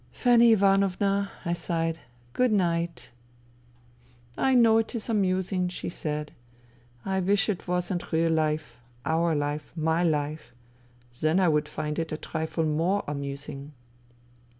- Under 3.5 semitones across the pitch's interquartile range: No, average, 4.2 semitones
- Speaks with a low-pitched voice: No, medium, 165 Hz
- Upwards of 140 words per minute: Yes, average, 150 wpm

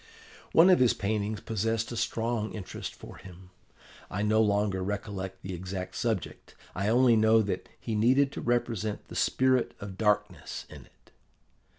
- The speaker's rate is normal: Yes, average, 160 wpm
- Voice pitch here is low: Yes, low, 105 Hz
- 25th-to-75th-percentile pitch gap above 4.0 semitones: No, average, 2.7 semitones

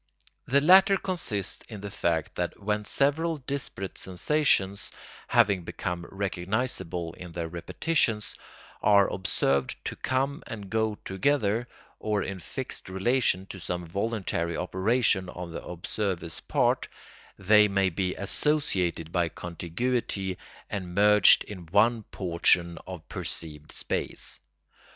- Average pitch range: Yes, average, 4.3 semitones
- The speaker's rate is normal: No, slow, 120 wpm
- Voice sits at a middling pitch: No, very low, 95 Hz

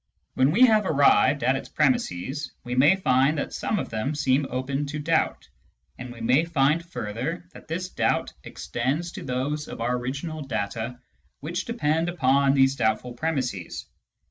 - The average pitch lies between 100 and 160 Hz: Yes, medium, 140 Hz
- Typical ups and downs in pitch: Yes, average, 4.3 semitones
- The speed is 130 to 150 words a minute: No, average, 165 wpm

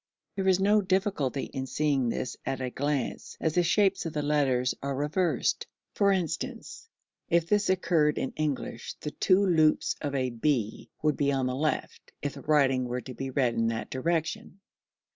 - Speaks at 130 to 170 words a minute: No, average, 195 wpm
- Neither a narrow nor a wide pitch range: Yes, average, 4.7 semitones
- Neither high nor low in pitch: Yes, medium, 150 Hz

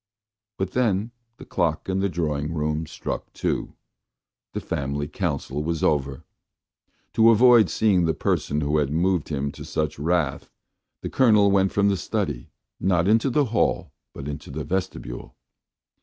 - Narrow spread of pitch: No, average, 5.3 semitones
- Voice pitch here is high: No, very low, 85 Hz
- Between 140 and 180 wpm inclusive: Yes, average, 155 wpm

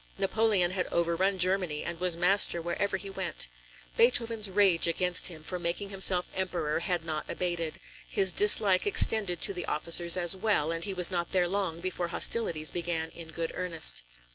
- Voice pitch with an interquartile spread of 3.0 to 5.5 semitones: No, narrow, 2.5 semitones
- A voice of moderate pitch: Yes, medium, 180 Hz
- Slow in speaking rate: No, average, 170 wpm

